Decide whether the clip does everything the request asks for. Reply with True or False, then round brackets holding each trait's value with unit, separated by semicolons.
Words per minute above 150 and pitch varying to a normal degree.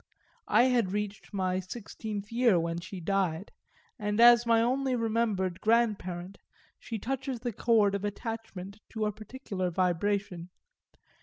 False (135 wpm; 3.7 semitones)